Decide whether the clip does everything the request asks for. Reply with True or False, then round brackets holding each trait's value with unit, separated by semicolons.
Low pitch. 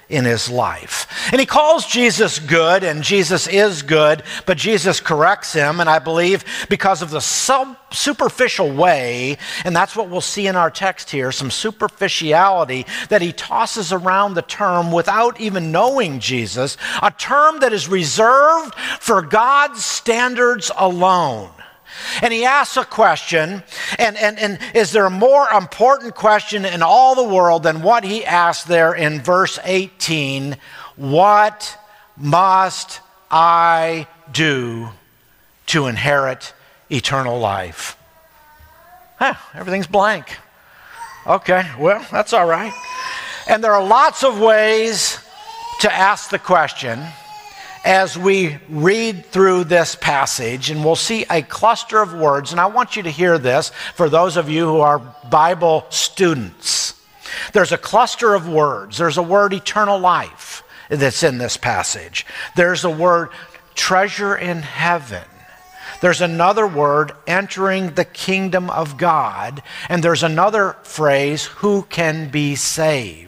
False (185 Hz)